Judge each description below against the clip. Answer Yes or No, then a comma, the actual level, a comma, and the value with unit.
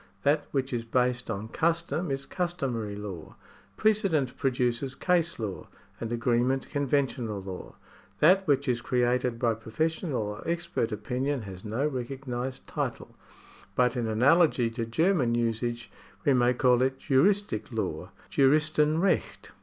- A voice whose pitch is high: No, low, 125 Hz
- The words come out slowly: Yes, slow, 130 wpm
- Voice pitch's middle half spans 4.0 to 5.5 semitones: Yes, average, 4.4 semitones